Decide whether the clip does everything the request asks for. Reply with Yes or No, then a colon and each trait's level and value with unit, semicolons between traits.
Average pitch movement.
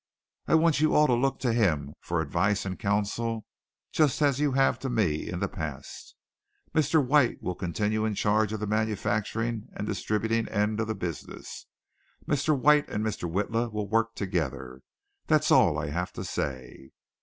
Yes: average, 4.2 semitones